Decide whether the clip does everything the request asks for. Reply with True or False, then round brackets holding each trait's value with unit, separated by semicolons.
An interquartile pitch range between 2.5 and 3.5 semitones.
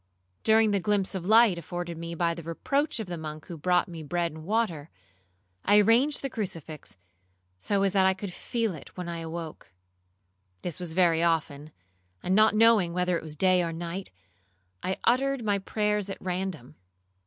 False (3.9 semitones)